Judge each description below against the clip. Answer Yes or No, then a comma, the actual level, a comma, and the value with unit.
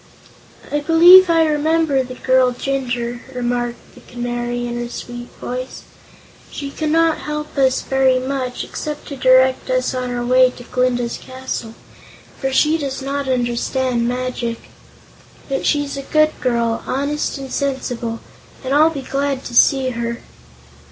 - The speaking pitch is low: No, very high, 260 Hz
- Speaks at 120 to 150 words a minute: Yes, average, 145 wpm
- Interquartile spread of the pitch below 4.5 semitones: Yes, narrow, 2.6 semitones